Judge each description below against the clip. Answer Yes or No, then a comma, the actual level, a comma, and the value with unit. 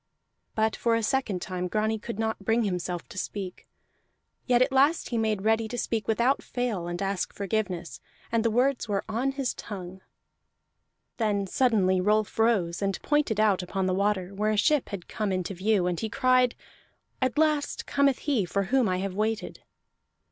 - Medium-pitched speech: No, high, 215 Hz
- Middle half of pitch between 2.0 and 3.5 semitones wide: No, average, 3.9 semitones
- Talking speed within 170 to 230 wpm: Yes, average, 180 wpm